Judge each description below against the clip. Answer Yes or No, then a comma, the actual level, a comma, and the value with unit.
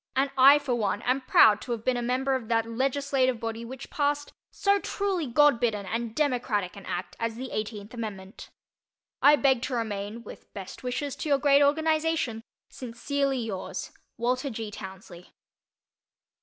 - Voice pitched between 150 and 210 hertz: No, high, 245 Hz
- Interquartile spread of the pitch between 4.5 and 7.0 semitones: No, average, 4.0 semitones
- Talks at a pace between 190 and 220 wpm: No, average, 165 wpm